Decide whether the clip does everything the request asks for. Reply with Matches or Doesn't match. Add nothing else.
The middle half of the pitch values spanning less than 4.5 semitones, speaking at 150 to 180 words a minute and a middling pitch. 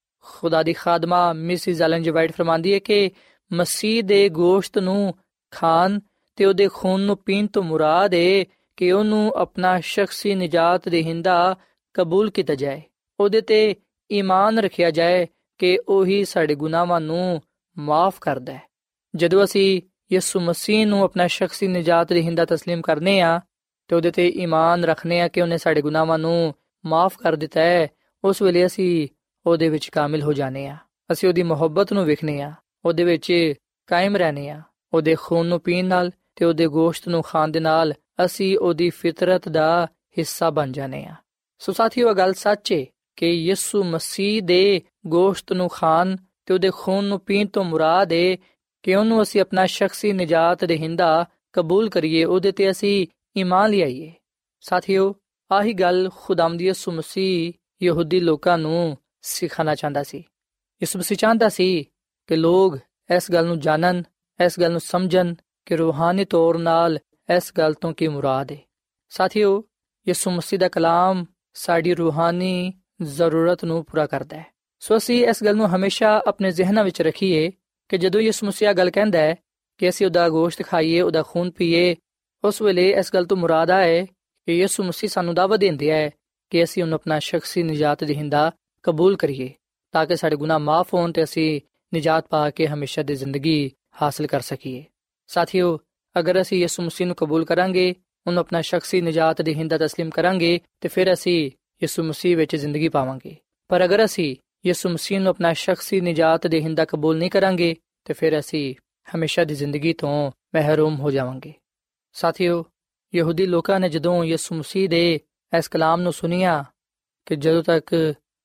Matches